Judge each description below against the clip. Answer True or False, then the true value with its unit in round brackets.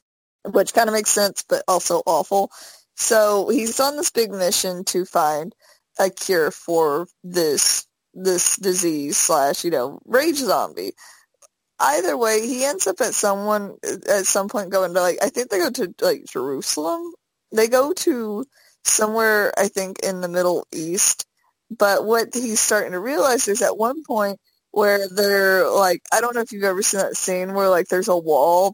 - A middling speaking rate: True (175 wpm)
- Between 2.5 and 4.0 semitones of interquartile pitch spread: True (3.5 semitones)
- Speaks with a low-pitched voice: False (200 Hz)